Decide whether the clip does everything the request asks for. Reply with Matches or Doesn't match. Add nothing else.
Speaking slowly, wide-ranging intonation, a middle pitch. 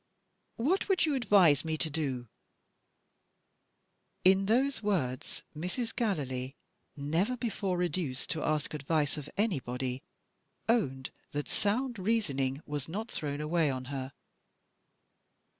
Matches